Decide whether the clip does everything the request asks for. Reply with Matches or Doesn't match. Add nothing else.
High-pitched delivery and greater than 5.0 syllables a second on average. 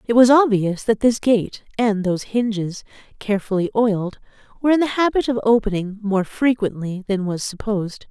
Matches